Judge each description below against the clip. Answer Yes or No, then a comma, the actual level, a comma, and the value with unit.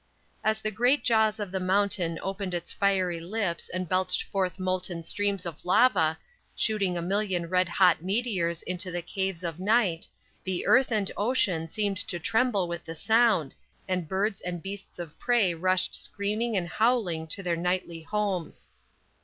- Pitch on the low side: No, medium, 185 Hz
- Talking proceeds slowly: No, average, 165 wpm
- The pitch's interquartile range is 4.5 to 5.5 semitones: No, average, 3.3 semitones